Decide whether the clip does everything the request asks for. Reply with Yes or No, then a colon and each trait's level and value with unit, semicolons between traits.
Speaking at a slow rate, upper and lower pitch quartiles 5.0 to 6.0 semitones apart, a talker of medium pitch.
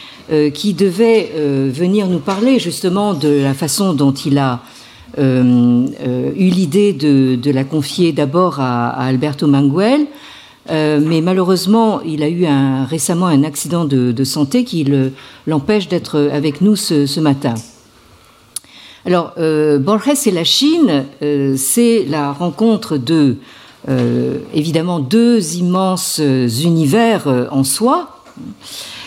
Yes: slow, 140 wpm; average, 5.3 semitones; medium, 155 Hz